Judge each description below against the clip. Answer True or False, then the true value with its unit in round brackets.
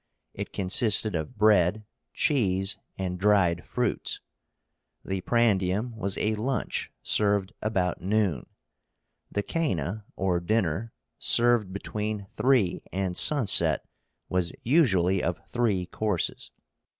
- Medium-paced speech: False (105 wpm)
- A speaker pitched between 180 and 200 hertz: False (100 Hz)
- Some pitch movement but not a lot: True (3.2 semitones)